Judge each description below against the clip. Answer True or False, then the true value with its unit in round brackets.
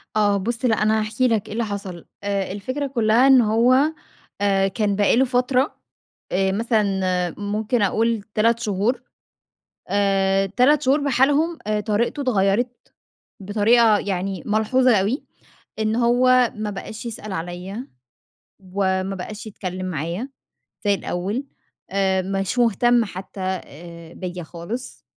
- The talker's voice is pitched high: True (210 Hz)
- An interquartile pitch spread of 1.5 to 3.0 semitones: False (3.8 semitones)